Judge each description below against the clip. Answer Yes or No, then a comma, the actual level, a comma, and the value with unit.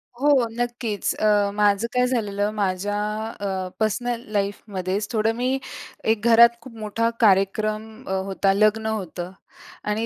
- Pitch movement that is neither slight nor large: No, narrow, 2.3 semitones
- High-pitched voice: Yes, high, 215 Hz